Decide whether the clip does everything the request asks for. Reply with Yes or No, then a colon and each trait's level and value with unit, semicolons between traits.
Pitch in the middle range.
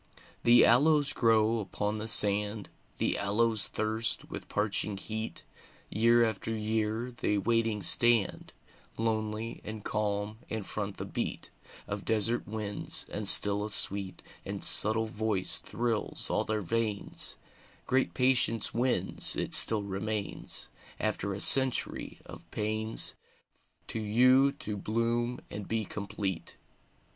No: low, 110 Hz